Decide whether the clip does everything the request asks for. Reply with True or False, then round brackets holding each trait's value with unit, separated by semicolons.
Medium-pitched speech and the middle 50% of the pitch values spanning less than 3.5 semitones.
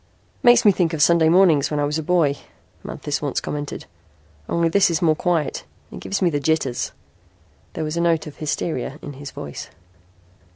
True (160 Hz; 2.7 semitones)